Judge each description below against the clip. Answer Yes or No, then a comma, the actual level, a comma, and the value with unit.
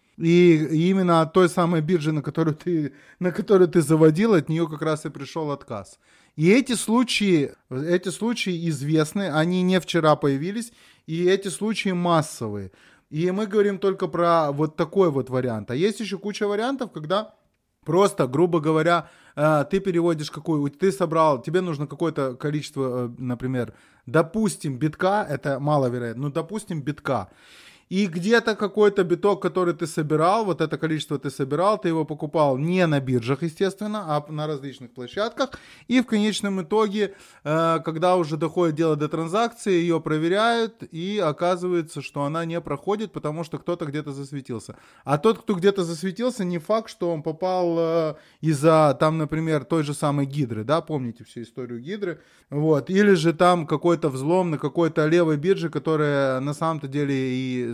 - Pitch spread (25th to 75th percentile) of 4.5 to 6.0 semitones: No, average, 4.0 semitones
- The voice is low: No, medium, 165 Hz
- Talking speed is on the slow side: No, fast, 160 wpm